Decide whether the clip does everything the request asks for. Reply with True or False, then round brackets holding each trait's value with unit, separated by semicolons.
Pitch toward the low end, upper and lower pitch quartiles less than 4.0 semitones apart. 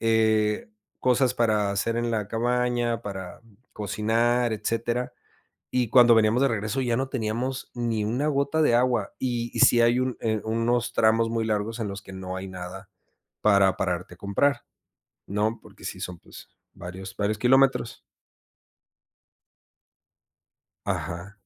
True (115 Hz; 2.8 semitones)